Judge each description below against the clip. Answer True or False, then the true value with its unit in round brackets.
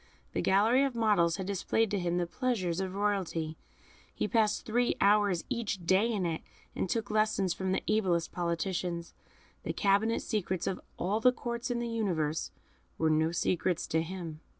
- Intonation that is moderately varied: True (4.1 semitones)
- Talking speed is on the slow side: False (175 wpm)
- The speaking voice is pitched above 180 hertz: True (190 Hz)